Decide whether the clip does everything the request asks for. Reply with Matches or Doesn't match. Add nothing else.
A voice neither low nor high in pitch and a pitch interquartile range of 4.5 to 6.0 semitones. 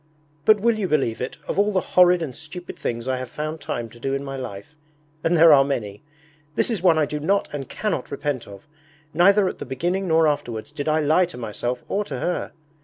Matches